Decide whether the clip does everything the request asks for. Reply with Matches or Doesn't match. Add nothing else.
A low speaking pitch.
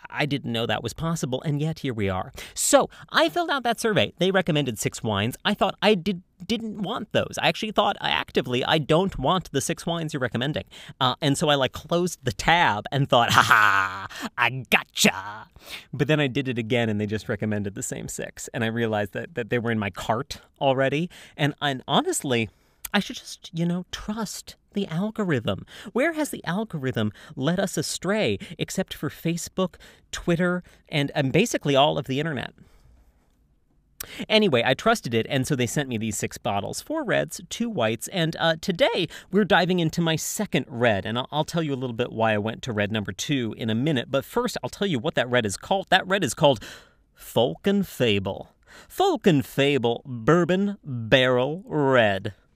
Doesn't match